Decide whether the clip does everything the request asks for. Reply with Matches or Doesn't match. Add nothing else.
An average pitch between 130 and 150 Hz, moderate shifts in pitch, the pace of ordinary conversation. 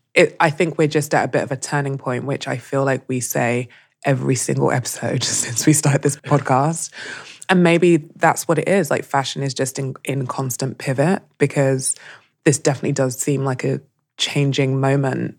Doesn't match